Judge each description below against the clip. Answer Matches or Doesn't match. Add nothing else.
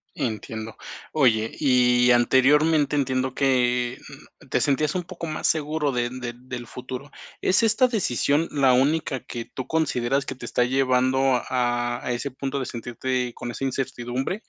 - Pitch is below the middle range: Matches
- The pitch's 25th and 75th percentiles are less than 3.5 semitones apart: Matches